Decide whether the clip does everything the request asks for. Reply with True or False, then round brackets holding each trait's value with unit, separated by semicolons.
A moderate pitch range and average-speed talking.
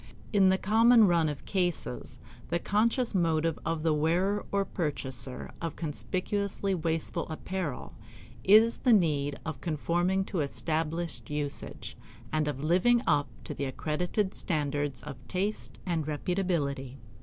False (4.4 semitones; 130 wpm)